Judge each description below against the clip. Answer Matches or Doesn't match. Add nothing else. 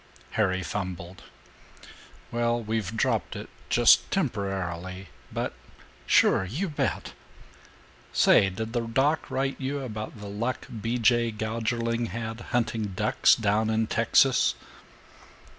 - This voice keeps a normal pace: Doesn't match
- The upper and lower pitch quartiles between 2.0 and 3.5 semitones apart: Matches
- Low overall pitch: Matches